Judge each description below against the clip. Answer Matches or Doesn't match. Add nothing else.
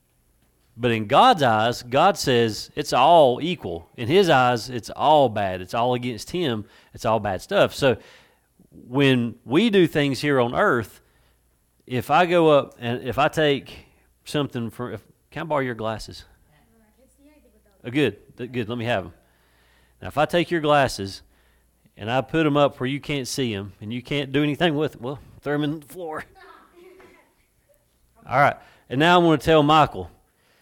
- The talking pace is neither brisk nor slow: Matches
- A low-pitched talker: Matches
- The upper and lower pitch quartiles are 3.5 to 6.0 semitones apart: Matches